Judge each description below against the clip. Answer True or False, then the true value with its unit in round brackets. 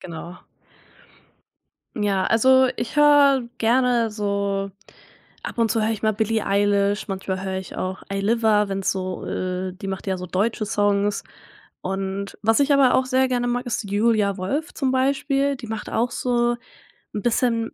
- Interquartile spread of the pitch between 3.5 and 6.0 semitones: True (3.8 semitones)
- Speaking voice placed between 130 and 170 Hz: False (215 Hz)